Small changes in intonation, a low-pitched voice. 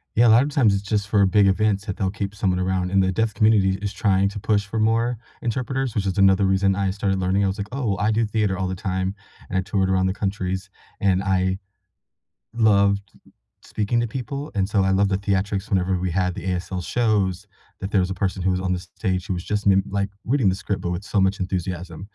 Yes: narrow, 1.9 semitones; low, 100 Hz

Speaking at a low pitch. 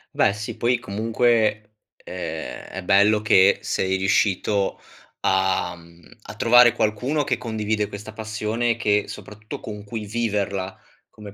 Yes: low, 105 Hz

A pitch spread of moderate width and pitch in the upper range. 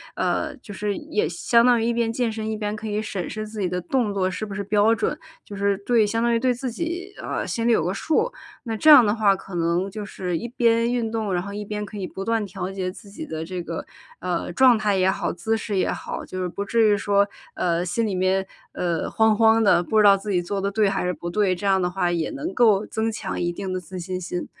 Yes: average, 3.5 semitones; high, 205 Hz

